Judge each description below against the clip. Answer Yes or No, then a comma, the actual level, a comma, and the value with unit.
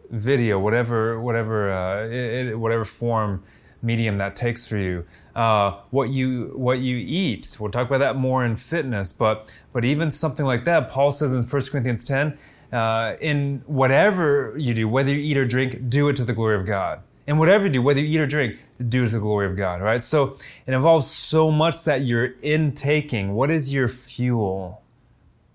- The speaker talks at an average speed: Yes, average, 195 wpm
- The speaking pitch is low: Yes, low, 125 Hz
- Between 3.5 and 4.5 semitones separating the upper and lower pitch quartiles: Yes, average, 4.2 semitones